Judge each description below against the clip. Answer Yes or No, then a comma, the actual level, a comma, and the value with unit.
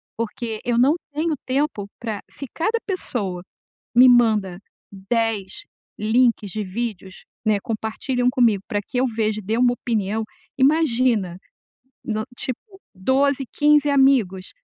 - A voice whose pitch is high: Yes, high, 230 Hz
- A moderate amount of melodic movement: Yes, average, 4.0 semitones